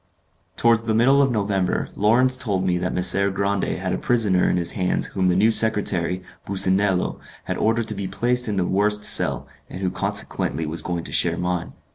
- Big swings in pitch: No, average, 3.4 semitones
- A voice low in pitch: Yes, low, 100 Hz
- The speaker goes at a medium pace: Yes, average, 195 wpm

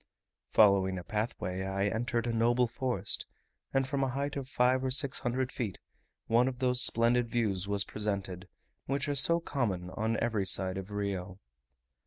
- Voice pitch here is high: No, low, 115 Hz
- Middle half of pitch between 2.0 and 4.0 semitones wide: No, average, 4.6 semitones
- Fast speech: No, average, 170 wpm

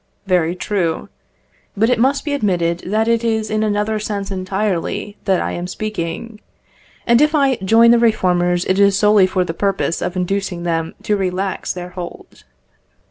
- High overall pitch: Yes, high, 195 Hz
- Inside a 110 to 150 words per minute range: No, average, 170 wpm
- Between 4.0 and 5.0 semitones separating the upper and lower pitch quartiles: No, average, 3.3 semitones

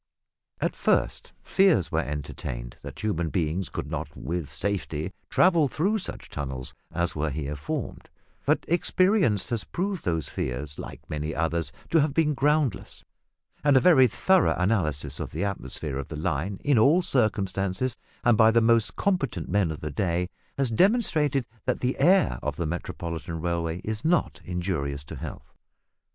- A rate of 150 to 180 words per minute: Yes, average, 160 wpm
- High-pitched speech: No, very low, 95 Hz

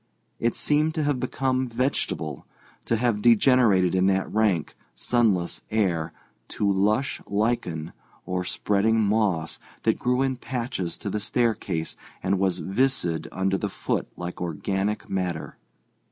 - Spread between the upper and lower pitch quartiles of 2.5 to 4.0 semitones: No, average, 4.7 semitones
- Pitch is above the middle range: No, low, 105 Hz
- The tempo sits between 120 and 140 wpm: Yes, slow, 135 wpm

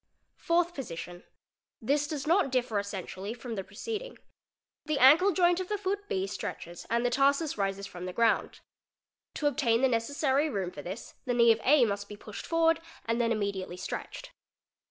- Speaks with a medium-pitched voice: No, high, 245 Hz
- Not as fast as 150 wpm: No, average, 175 wpm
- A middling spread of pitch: No, wide, 7.3 semitones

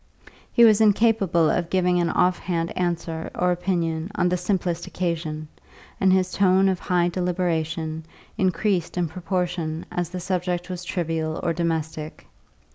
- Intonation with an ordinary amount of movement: No, narrow, 1.9 semitones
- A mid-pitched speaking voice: Yes, medium, 175 Hz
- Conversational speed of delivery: Yes, average, 145 wpm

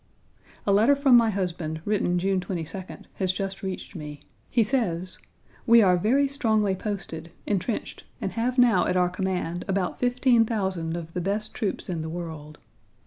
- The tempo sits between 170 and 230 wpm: No, average, 160 wpm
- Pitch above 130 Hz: Yes, high, 190 Hz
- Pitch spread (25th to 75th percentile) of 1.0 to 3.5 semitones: No, average, 4.2 semitones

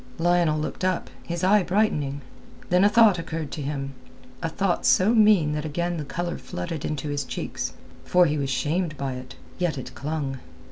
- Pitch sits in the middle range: Yes, medium, 165 Hz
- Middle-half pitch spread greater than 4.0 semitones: No, average, 3.7 semitones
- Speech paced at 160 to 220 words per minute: Yes, average, 185 wpm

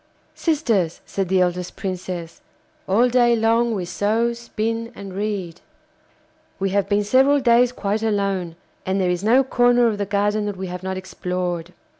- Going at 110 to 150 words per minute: No, average, 165 wpm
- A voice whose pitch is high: Yes, high, 205 Hz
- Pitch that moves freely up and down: No, average, 3.9 semitones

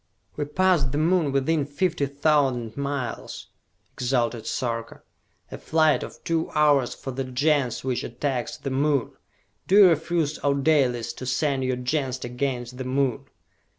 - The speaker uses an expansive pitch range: No, average, 3.3 semitones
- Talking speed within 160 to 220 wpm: No, average, 150 wpm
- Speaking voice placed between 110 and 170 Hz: Yes, medium, 140 Hz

